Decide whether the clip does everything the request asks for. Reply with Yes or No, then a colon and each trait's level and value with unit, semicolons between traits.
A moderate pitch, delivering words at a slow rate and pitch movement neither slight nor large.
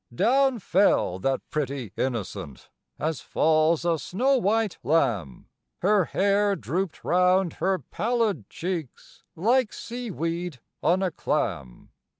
No: medium, 175 Hz; slow, 120 wpm; wide, 6.3 semitones